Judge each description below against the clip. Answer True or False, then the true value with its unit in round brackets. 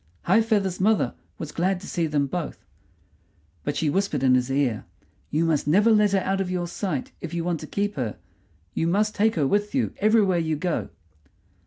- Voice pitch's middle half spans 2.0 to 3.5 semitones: False (4.9 semitones)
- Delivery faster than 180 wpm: True (200 wpm)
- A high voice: False (180 Hz)